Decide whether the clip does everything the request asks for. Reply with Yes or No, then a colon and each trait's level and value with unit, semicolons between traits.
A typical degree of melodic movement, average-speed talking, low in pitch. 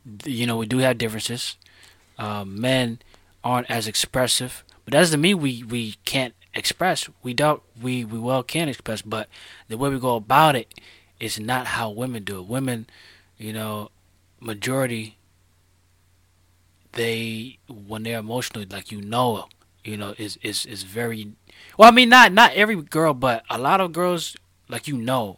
Yes: average, 4.1 semitones; average, 170 wpm; low, 115 Hz